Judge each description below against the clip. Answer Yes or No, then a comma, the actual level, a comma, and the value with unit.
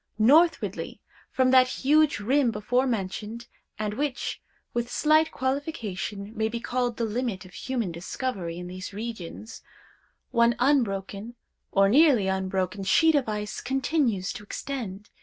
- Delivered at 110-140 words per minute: Yes, slow, 135 wpm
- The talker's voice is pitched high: Yes, high, 230 Hz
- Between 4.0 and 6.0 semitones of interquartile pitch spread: Yes, average, 4.8 semitones